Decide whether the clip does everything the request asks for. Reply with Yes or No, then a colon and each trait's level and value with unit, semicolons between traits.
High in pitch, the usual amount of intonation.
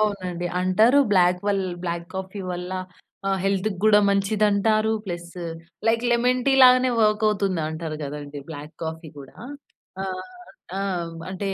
Yes: high, 195 Hz; average, 3.6 semitones